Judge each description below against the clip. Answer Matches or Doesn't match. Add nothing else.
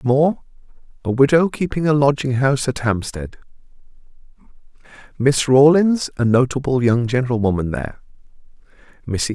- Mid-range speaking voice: Doesn't match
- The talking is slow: Matches